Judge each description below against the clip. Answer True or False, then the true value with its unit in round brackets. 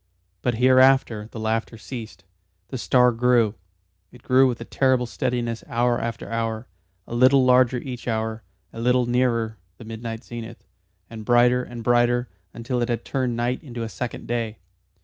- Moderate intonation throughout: False (1.6 semitones)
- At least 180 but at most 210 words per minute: False (165 wpm)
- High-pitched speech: False (120 Hz)